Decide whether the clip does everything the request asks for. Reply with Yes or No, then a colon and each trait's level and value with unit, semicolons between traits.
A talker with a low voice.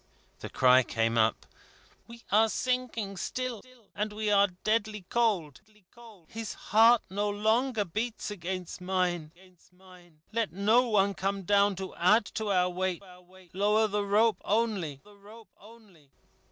No: high, 205 Hz